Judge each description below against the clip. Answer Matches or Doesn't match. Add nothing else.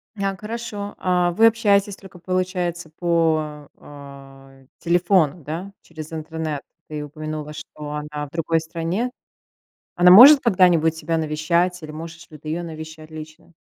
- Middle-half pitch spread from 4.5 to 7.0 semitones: Doesn't match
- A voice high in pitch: Doesn't match